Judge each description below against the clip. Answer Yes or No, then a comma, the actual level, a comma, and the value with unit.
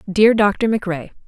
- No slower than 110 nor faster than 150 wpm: Yes, average, 140 wpm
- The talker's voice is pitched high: Yes, high, 200 Hz